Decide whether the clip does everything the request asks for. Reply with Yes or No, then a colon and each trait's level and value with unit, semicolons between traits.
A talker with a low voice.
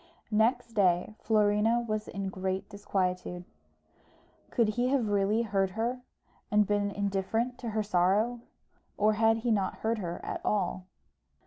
No: high, 210 Hz